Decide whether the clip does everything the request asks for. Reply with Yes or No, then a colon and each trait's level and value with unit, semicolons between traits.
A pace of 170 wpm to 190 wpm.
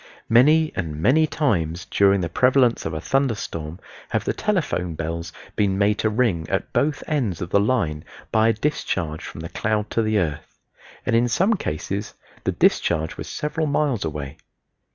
Yes: average, 175 wpm